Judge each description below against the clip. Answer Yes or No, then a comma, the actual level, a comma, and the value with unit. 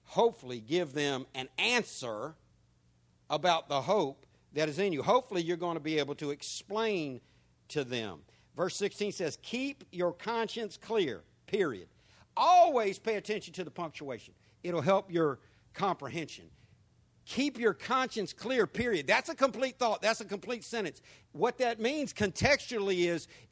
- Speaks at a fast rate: No, average, 150 wpm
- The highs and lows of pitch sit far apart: Yes, wide, 7.7 semitones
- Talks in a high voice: No, medium, 175 Hz